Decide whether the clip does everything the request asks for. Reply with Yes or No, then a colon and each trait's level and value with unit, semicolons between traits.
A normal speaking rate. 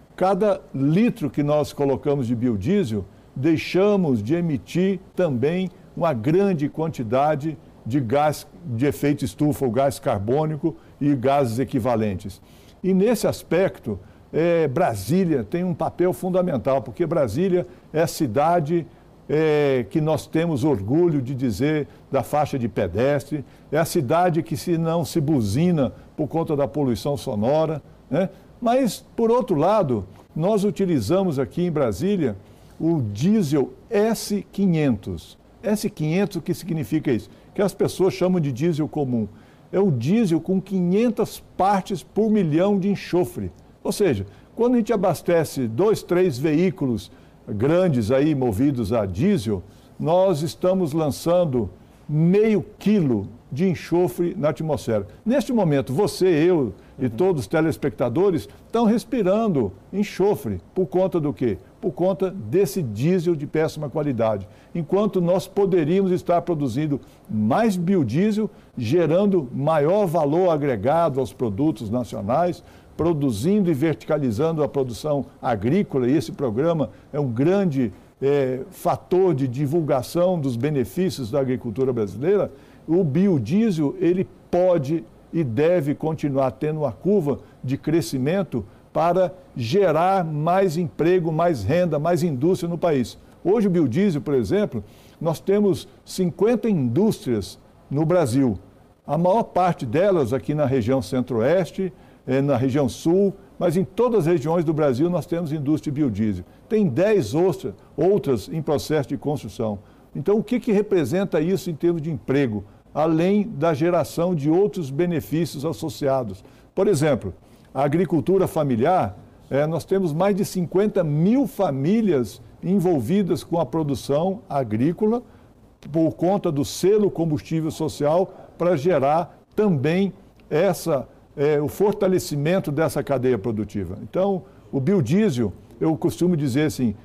Yes: average, 130 wpm